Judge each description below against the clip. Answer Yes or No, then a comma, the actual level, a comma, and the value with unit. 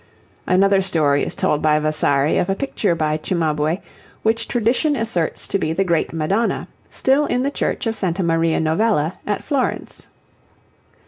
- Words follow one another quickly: No, average, 155 wpm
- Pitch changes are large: Yes, wide, 6.1 semitones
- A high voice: No, medium, 180 Hz